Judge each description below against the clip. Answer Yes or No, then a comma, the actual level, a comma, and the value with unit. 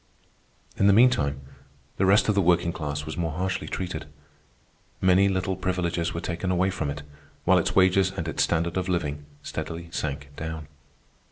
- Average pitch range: Yes, average, 3.0 semitones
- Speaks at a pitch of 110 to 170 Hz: No, very low, 85 Hz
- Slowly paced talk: No, average, 170 wpm